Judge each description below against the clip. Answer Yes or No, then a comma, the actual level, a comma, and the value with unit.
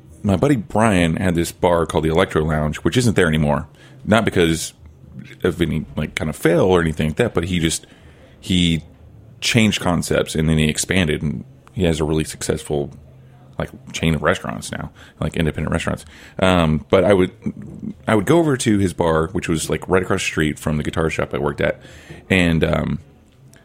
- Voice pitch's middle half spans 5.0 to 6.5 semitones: No, average, 3.3 semitones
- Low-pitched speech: Yes, very low, 80 Hz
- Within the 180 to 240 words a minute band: Yes, average, 195 wpm